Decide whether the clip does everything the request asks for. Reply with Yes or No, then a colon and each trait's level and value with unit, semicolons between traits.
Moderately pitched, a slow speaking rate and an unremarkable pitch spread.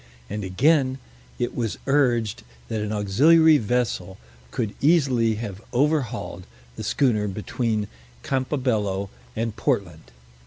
No: low, 115 Hz; slow, 110 wpm; average, 4.5 semitones